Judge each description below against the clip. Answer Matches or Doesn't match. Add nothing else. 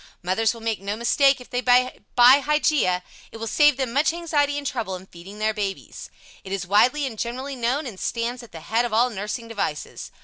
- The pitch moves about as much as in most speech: Matches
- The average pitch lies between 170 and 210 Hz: Doesn't match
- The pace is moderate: Doesn't match